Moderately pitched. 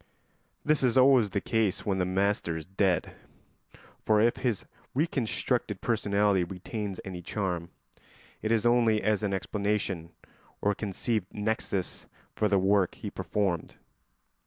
No: low, 105 Hz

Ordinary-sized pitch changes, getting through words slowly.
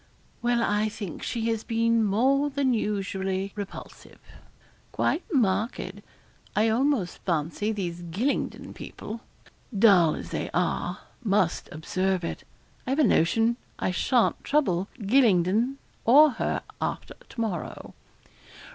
Yes: average, 4.0 semitones; slow, 120 wpm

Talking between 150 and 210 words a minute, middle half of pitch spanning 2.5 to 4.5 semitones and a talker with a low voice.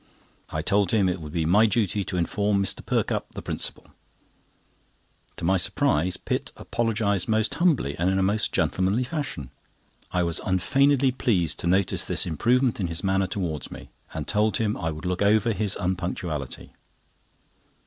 Yes: average, 165 wpm; average, 3.8 semitones; very low, 95 Hz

